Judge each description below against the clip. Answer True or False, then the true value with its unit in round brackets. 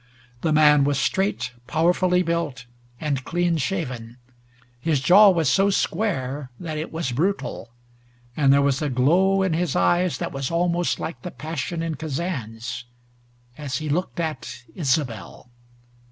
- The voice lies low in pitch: False (155 Hz)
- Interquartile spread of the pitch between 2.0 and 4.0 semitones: False (4.6 semitones)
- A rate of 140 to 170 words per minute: True (145 wpm)